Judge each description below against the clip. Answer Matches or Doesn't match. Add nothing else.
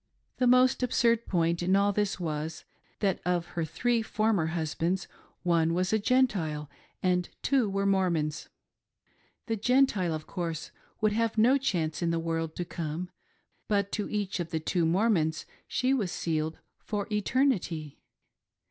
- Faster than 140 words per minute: Matches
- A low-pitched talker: Doesn't match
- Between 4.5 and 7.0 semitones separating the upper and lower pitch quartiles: Matches